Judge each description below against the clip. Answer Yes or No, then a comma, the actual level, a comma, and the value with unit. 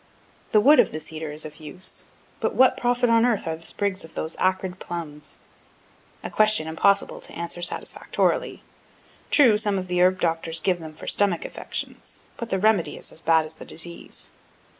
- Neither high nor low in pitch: Yes, medium, 180 Hz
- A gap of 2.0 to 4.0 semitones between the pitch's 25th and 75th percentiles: No, average, 4.4 semitones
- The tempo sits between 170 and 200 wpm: Yes, average, 185 wpm